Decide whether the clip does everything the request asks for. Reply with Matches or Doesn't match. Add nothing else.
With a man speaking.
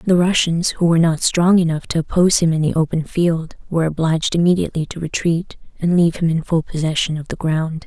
Doesn't match